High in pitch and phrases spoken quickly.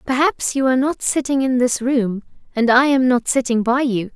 Yes: very high, 255 Hz; fast, 215 wpm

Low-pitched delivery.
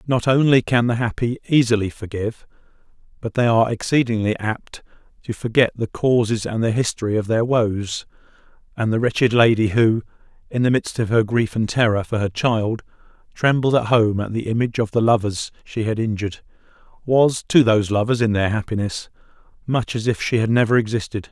Yes: low, 115 Hz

